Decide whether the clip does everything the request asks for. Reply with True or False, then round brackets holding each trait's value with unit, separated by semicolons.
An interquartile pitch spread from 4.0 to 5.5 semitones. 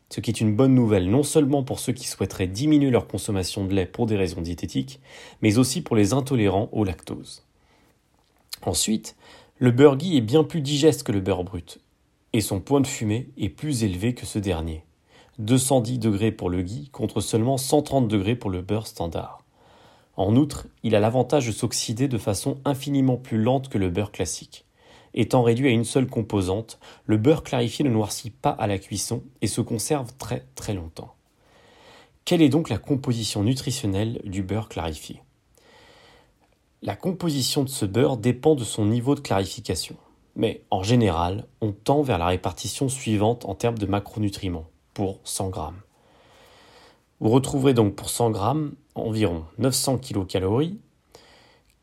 True (4.9 semitones)